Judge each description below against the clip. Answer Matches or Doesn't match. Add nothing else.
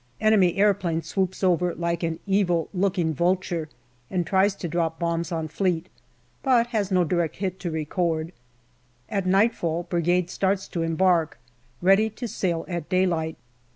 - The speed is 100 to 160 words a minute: Matches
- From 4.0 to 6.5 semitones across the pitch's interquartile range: Doesn't match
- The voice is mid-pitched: Matches